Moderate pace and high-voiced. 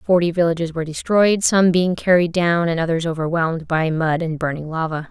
No: average, 190 wpm; medium, 170 Hz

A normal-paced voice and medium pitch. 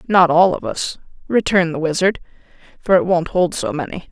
Yes: average, 190 wpm; medium, 180 Hz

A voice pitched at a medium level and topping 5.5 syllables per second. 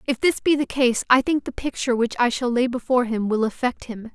No: high, 245 Hz; 5.9 syllables/s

